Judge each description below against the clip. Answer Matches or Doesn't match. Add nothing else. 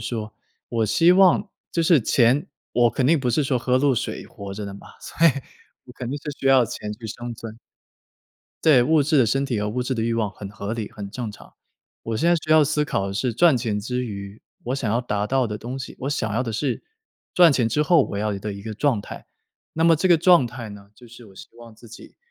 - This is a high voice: Doesn't match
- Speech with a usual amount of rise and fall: Matches